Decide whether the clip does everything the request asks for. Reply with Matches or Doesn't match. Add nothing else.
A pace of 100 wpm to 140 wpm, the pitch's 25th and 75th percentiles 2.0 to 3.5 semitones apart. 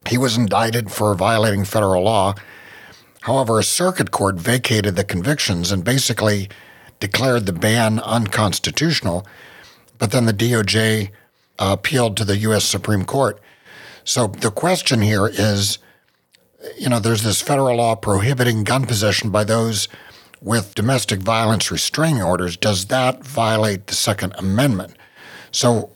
Matches